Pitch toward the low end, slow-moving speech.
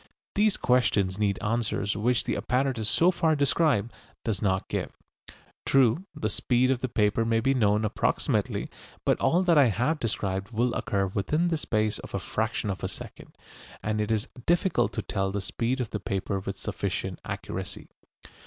No: low, 115 Hz; average, 175 wpm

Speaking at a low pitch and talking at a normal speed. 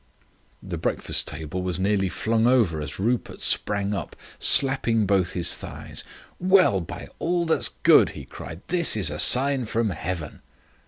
Yes: low, 105 Hz; average, 155 wpm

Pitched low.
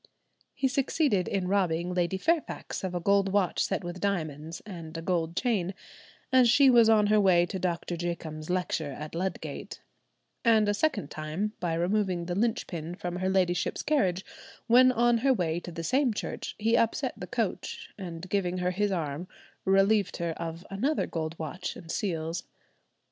No: medium, 185 Hz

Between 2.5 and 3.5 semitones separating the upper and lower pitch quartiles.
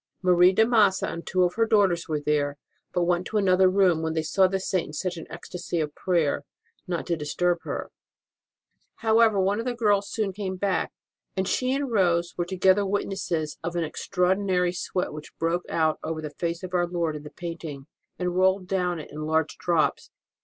Yes: average, 2.8 semitones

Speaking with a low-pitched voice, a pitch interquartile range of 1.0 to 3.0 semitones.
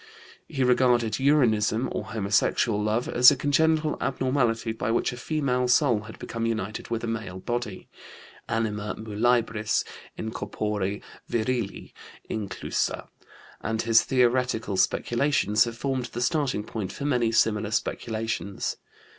Yes: low, 115 Hz; average, 2.7 semitones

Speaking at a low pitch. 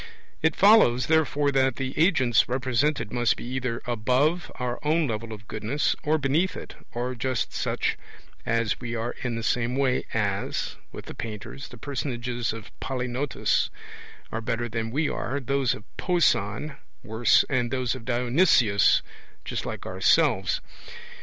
Yes: low, 125 Hz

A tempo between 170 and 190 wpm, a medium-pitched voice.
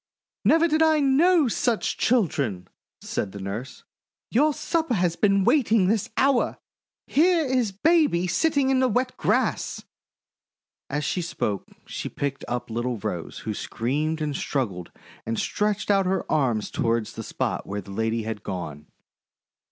No: average, 150 wpm; medium, 180 Hz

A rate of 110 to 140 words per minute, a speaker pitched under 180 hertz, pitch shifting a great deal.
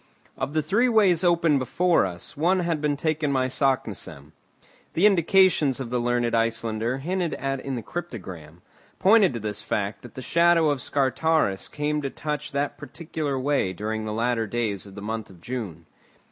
No: average, 175 wpm; low, 135 Hz; wide, 6.1 semitones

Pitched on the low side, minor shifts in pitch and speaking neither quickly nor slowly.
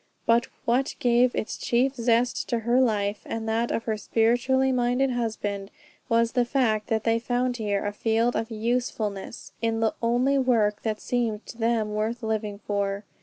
No: high, 230 Hz; narrow, 2.1 semitones; average, 170 wpm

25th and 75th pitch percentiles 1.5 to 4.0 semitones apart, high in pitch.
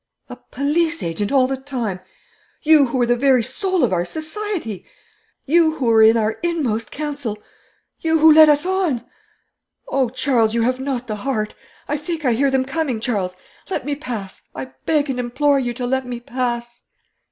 No: average, 4.4 semitones; very high, 260 Hz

